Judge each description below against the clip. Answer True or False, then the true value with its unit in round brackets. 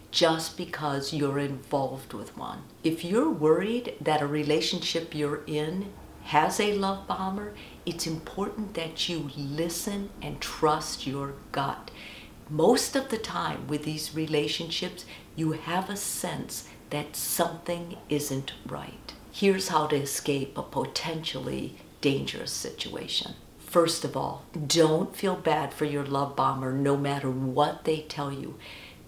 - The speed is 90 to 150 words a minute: True (135 wpm)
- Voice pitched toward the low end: False (155 Hz)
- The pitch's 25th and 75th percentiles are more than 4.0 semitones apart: False (3.2 semitones)